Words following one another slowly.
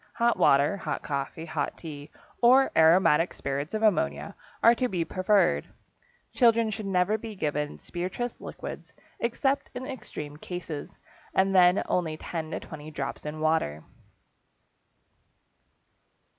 Yes: slow, 130 wpm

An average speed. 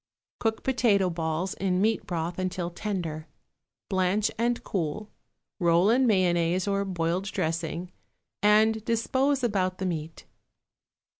No: slow, 120 wpm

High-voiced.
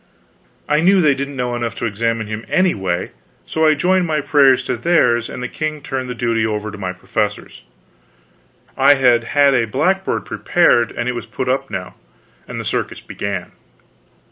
No: low, 125 Hz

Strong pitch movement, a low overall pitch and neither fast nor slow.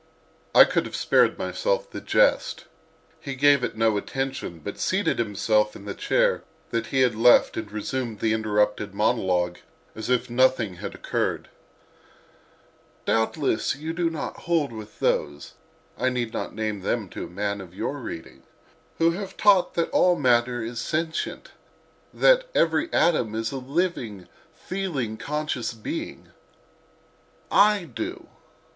Yes: wide, 6.3 semitones; low, 120 Hz; average, 145 wpm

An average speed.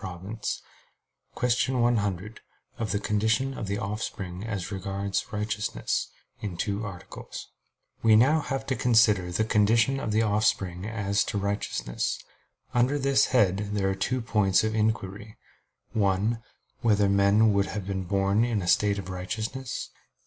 Yes: average, 145 wpm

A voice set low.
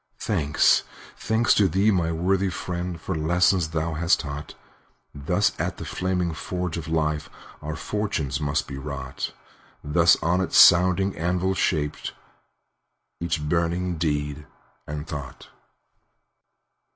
Yes: very low, 85 Hz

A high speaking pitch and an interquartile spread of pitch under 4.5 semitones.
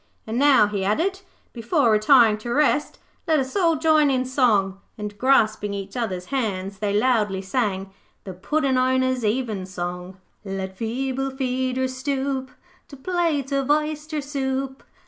No: very high, 255 Hz; average, 4.9 semitones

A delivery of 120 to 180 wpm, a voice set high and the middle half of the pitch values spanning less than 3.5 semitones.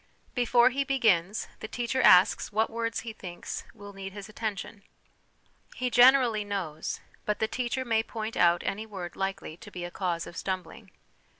No: average, 170 wpm; high, 215 Hz; average, 3.9 semitones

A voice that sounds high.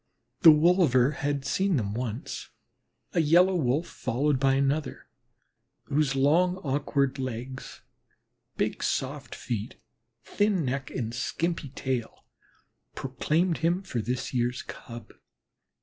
No: medium, 140 Hz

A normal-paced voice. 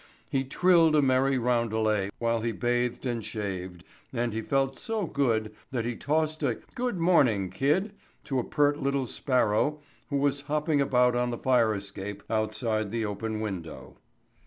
Yes: average, 160 wpm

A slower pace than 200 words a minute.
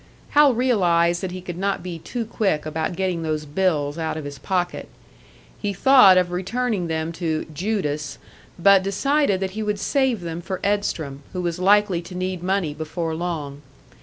Yes: average, 175 wpm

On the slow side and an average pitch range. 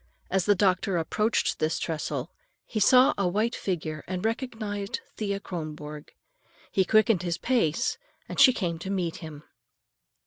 No: average, 145 wpm; average, 4.6 semitones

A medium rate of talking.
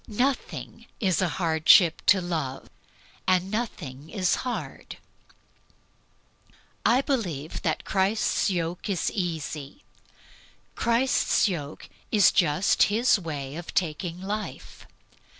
No: slow, 100 wpm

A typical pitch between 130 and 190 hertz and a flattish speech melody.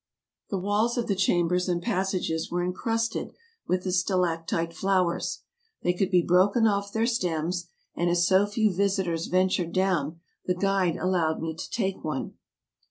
Yes: medium, 185 Hz; narrow, 2.3 semitones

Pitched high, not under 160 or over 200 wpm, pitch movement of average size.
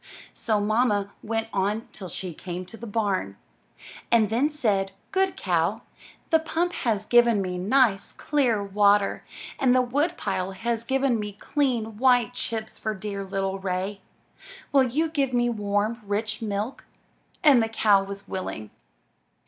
No: high, 220 Hz; average, 150 wpm; average, 3.7 semitones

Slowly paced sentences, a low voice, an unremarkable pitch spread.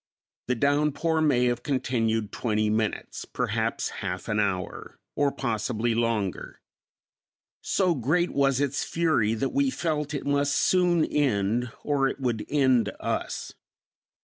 Yes: slow, 130 wpm; low, 130 Hz; average, 4.7 semitones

